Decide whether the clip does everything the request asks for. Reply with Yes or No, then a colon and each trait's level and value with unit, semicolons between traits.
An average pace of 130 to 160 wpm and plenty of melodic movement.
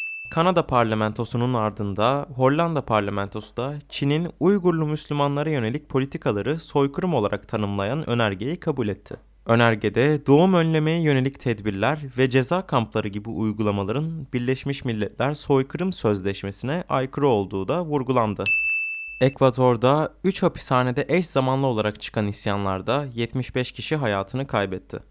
No: average, 110 wpm; wide, 5.8 semitones